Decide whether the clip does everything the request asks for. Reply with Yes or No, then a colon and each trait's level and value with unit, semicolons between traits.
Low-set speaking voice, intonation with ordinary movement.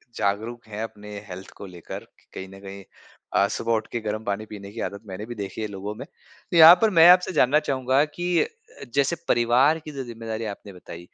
Yes: low, 110 Hz; average, 4.6 semitones